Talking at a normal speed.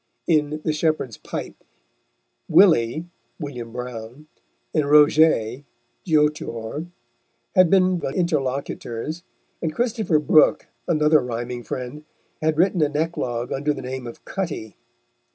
No: slow, 120 wpm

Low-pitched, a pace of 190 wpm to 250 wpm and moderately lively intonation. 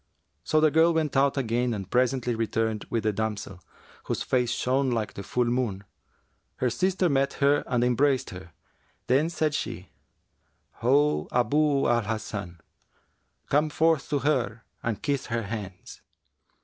No: low, 125 Hz; average, 150 wpm; average, 4.4 semitones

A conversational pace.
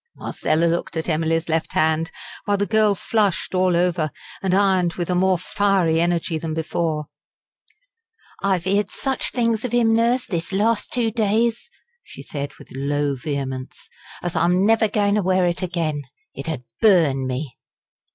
Yes: average, 160 wpm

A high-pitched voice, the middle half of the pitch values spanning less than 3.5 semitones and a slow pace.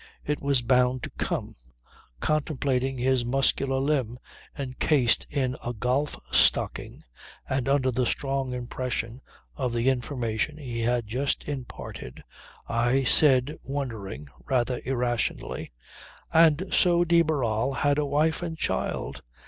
No: low, 130 Hz; average, 2.7 semitones; slow, 125 wpm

